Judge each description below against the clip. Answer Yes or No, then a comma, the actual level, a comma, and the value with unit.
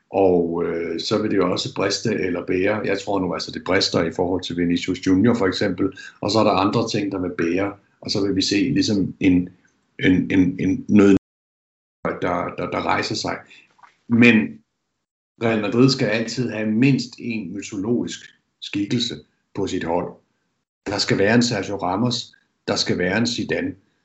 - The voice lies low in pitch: Yes, low, 100 Hz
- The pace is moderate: Yes, average, 180 wpm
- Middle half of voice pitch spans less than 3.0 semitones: No, average, 4.4 semitones